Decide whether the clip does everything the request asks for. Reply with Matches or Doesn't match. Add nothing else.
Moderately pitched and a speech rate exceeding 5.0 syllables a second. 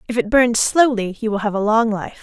Doesn't match